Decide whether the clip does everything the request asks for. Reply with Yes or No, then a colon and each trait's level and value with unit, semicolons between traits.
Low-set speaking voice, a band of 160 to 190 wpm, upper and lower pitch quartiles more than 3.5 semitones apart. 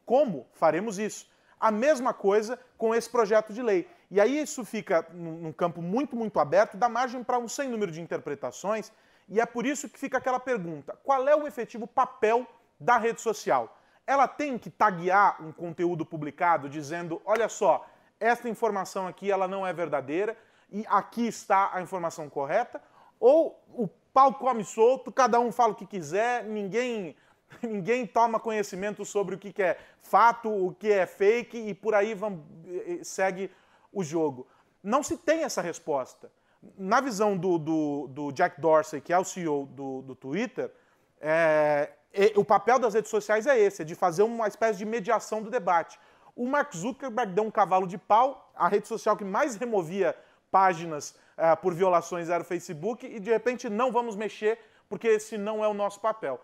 No: high, 215 Hz; average, 180 wpm; average, 4.5 semitones